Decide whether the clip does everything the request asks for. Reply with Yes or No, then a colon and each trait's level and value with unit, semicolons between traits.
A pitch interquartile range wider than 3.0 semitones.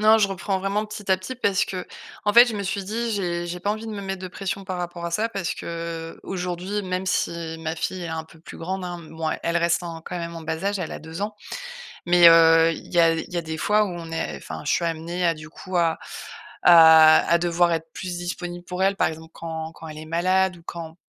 No: narrow, 2.6 semitones